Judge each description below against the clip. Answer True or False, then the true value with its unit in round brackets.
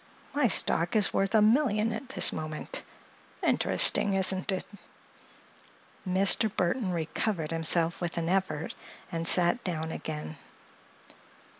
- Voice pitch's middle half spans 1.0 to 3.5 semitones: False (4.4 semitones)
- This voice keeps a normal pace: False (120 wpm)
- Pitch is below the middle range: False (185 Hz)